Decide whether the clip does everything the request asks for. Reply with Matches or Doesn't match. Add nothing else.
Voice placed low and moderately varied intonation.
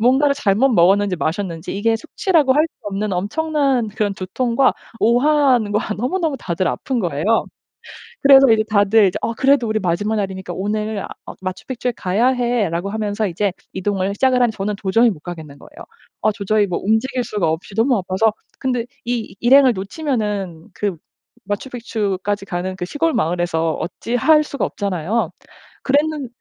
Doesn't match